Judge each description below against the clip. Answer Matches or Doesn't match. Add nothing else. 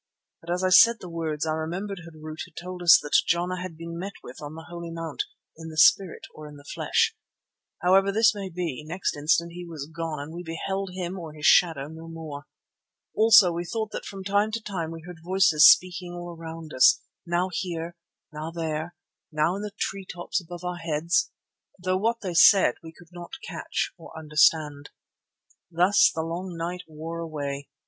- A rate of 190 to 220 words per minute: Matches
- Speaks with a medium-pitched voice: Matches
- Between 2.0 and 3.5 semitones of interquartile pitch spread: Matches